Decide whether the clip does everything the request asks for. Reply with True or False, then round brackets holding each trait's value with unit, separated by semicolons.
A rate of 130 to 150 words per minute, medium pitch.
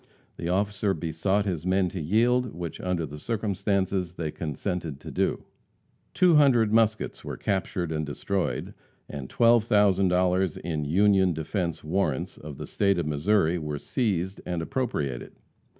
False (140 wpm; 90 Hz)